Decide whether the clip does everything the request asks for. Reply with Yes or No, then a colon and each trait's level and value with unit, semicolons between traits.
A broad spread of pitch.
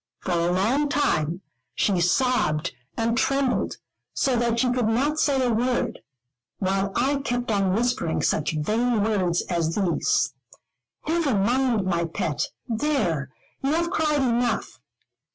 Yes: wide, 6.4 semitones